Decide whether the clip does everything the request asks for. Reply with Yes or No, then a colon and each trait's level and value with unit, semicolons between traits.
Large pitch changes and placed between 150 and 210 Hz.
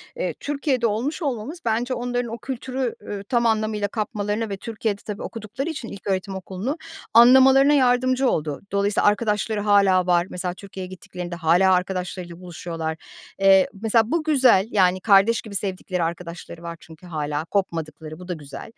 No: average, 4.8 semitones; high, 200 Hz